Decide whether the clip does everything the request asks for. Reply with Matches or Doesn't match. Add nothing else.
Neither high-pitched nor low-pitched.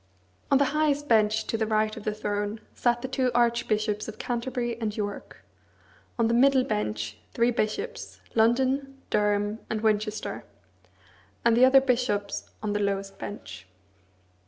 Doesn't match